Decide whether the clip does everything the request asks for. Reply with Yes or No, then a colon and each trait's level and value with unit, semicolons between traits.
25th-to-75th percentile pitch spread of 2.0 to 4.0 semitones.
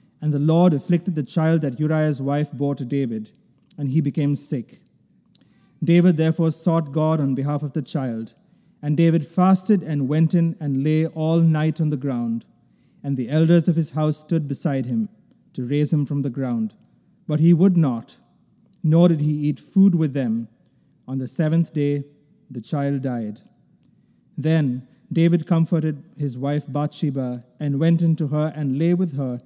Yes: average, 2.9 semitones